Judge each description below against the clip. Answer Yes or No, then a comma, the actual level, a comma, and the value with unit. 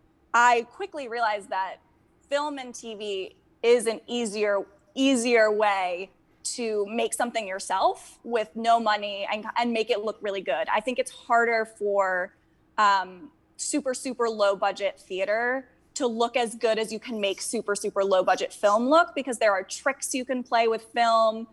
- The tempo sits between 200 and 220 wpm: No, average, 165 wpm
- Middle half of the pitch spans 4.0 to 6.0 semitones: No, average, 3.3 semitones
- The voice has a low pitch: No, high, 225 Hz